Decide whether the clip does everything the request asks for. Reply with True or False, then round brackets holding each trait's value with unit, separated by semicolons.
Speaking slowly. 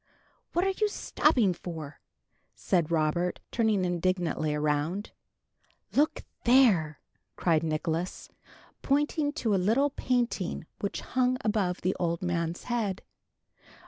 True (110 wpm)